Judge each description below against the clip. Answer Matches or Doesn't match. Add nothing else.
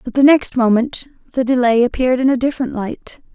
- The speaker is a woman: Matches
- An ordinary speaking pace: Matches